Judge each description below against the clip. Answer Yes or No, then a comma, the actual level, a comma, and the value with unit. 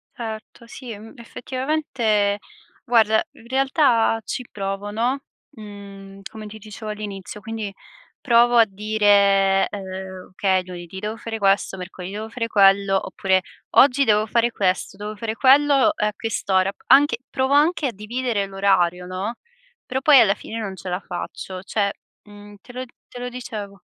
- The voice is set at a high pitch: Yes, high, 210 Hz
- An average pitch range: Yes, average, 3.3 semitones